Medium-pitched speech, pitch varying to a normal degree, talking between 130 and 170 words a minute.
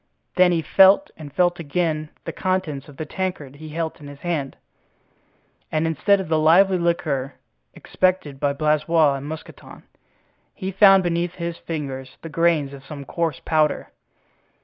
Yes: medium, 160 Hz; average, 3.4 semitones; average, 155 wpm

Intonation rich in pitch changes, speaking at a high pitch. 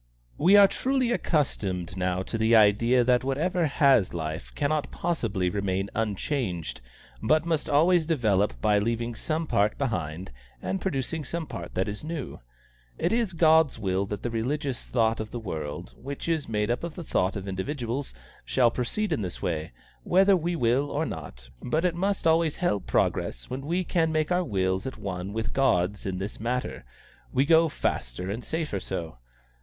No: wide, 8.5 semitones; low, 120 Hz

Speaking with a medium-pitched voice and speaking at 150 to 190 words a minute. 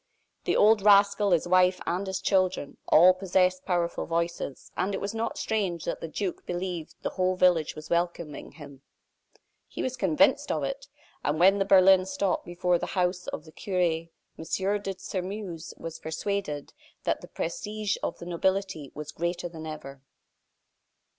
Yes: medium, 180 Hz; average, 165 wpm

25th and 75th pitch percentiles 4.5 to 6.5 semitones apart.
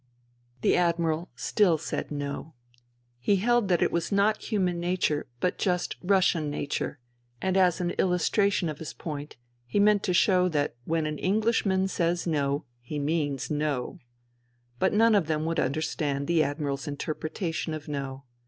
No: average, 4.1 semitones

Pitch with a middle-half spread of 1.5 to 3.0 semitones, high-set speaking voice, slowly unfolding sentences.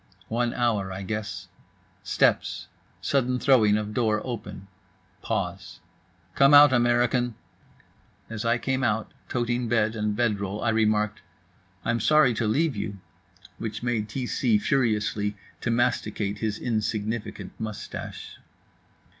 No: narrow, 2.5 semitones; low, 115 Hz; slow, 125 wpm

